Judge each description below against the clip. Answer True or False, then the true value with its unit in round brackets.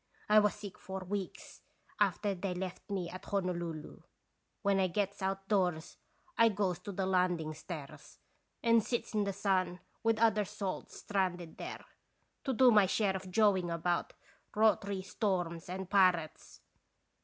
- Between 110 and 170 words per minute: True (155 wpm)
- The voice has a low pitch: False (190 Hz)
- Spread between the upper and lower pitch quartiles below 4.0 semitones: True (2.4 semitones)